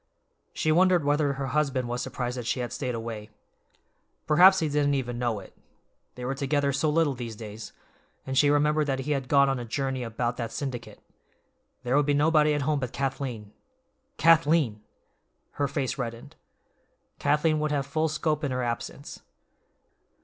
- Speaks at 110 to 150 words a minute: No, average, 170 wpm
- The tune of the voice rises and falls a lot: No, average, 3.5 semitones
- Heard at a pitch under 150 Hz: Yes, medium, 140 Hz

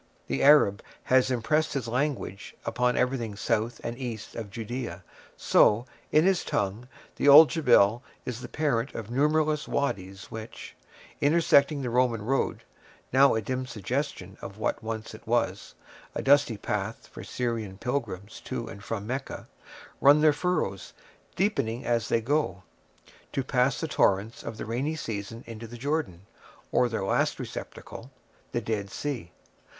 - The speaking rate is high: No, average, 145 wpm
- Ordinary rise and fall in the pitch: Yes, average, 4.4 semitones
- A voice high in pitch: No, low, 120 Hz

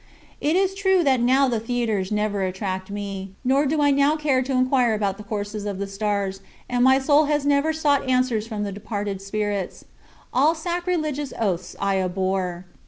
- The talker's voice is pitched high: Yes, high, 230 Hz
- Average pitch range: No, wide, 6.0 semitones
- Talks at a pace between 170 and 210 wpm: Yes, average, 180 wpm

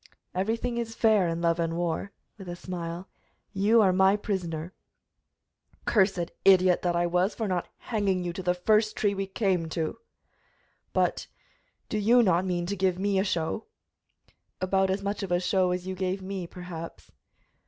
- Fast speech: No, average, 175 wpm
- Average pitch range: No, narrow, 2.3 semitones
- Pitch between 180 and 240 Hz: Yes, medium, 185 Hz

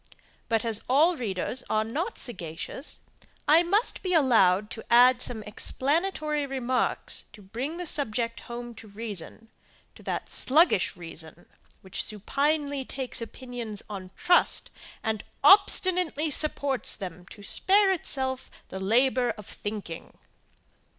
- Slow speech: Yes, slow, 125 wpm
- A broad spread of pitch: Yes, wide, 5.8 semitones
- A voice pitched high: Yes, high, 245 Hz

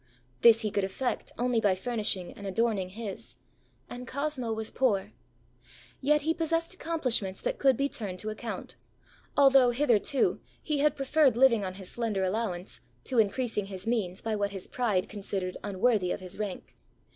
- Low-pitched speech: No, high, 225 Hz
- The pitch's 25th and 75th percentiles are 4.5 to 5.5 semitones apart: Yes, average, 4.9 semitones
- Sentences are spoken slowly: No, average, 165 wpm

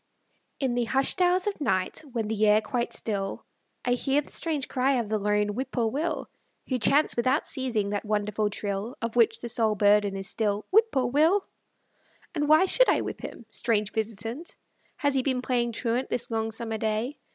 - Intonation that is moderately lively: Yes, average, 4.1 semitones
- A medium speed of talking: Yes, average, 185 wpm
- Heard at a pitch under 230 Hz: No, high, 235 Hz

